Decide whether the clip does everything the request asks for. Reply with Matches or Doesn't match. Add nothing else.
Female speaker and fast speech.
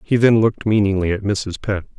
Doesn't match